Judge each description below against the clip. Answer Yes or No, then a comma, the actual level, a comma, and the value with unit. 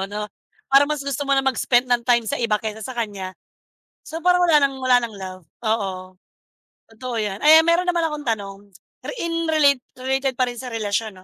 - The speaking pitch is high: Yes, very high, 255 Hz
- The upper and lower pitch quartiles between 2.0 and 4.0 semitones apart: No, average, 5.3 semitones